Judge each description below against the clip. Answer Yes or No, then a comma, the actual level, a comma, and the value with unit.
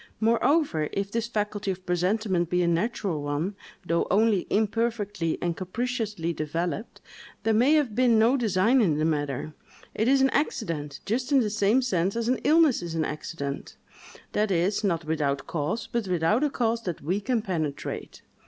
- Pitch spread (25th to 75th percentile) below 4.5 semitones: No, wide, 5.6 semitones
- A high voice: Yes, high, 200 Hz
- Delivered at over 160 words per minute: Yes, average, 170 wpm